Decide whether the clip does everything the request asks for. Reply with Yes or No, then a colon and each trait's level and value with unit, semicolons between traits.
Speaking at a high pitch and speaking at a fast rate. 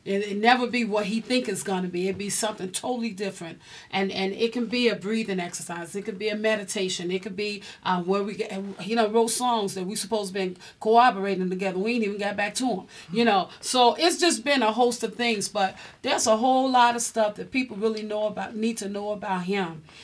Yes: high, 210 Hz; fast, 240 wpm